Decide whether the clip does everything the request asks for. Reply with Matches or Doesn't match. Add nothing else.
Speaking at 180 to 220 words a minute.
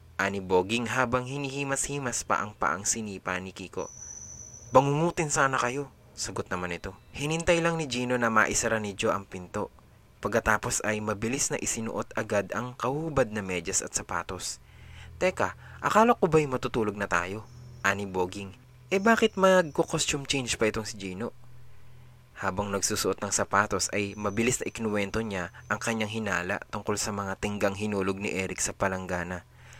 Doesn't match